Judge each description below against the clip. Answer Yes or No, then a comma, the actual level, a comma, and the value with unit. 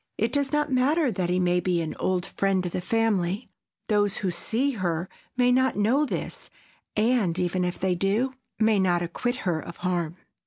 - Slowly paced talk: No, average, 185 wpm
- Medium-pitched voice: No, high, 195 Hz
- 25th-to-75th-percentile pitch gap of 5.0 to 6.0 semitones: Yes, wide, 5.4 semitones